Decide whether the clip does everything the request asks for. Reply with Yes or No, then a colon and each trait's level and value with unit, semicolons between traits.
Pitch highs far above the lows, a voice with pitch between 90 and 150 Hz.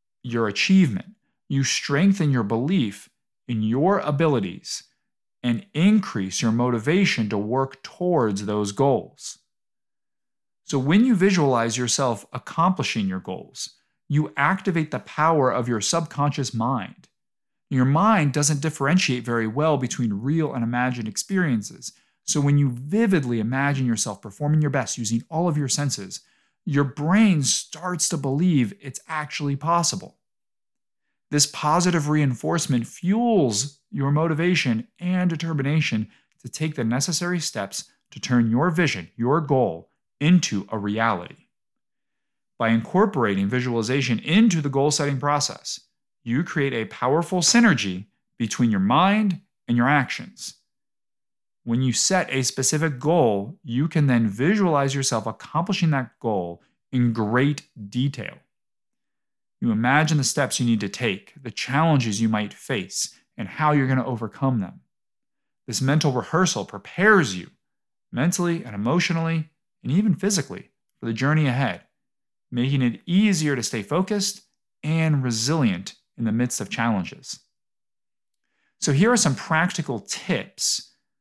Yes: wide, 5.7 semitones; medium, 140 Hz